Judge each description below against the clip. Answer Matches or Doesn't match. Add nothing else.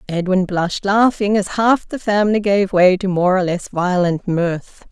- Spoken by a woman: Matches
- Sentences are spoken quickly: Doesn't match